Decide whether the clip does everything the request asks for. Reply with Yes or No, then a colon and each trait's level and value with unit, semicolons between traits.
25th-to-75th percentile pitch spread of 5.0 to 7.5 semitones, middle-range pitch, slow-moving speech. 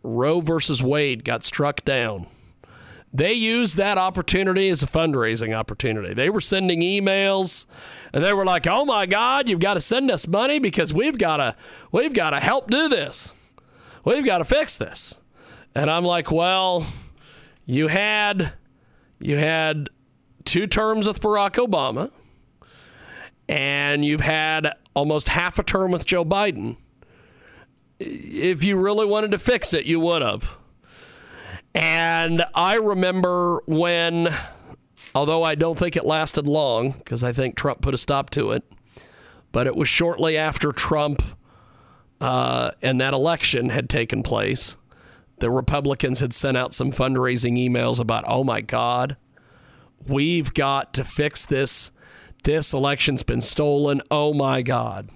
No: wide, 5.4 semitones; medium, 155 Hz; average, 150 wpm